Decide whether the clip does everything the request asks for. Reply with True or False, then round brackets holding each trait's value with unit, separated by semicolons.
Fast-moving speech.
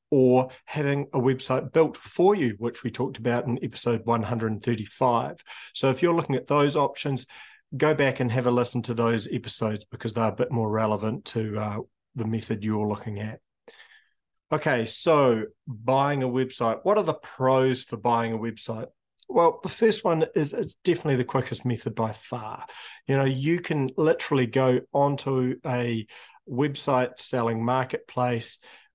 False (165 wpm)